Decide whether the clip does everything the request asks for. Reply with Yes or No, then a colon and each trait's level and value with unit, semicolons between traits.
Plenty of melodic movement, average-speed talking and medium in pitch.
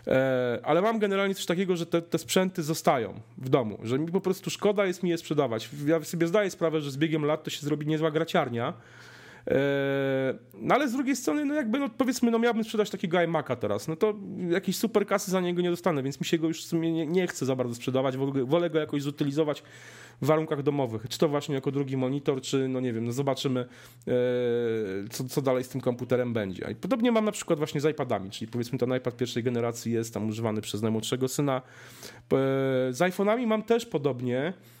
No: wide, 5.7 semitones; fast, 210 wpm; medium, 150 Hz